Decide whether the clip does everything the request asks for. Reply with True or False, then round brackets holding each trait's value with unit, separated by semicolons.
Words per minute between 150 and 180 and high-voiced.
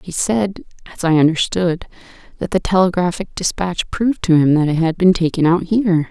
False (165 wpm; 175 Hz)